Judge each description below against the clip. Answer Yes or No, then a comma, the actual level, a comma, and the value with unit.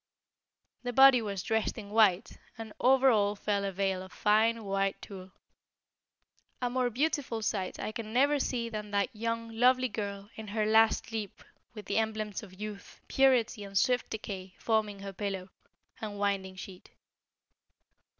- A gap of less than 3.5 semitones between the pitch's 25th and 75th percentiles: Yes, narrow, 2.5 semitones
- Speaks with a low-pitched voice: No, high, 215 Hz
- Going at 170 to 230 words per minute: No, average, 160 wpm